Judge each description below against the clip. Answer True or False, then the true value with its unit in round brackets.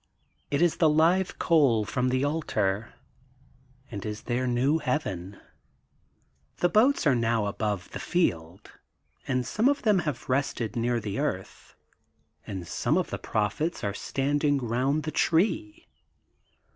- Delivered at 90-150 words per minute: True (140 wpm)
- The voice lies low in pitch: True (130 Hz)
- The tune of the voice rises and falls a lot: True (6.8 semitones)